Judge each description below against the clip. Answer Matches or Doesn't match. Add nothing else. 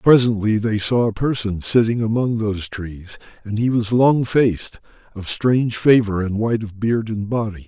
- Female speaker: Doesn't match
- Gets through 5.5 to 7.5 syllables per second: Doesn't match